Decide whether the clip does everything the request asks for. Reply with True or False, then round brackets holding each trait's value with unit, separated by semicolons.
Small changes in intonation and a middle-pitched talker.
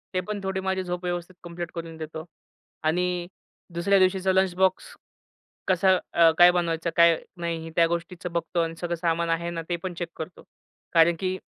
True (1.7 semitones; 175 Hz)